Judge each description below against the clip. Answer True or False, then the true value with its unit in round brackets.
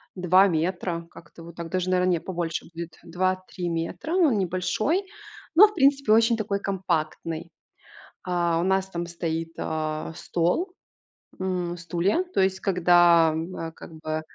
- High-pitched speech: False (175 Hz)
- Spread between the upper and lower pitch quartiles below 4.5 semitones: True (2.4 semitones)